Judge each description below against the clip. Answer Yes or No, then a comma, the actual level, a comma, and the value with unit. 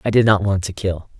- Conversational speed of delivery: No, fast, 300 wpm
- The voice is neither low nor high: No, low, 100 Hz